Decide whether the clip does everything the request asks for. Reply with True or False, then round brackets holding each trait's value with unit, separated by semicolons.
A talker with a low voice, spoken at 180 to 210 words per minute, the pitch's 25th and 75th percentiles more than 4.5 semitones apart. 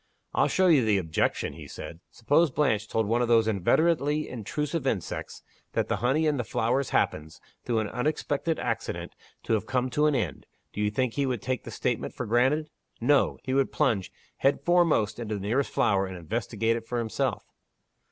True (120 Hz; 190 wpm; 4.9 semitones)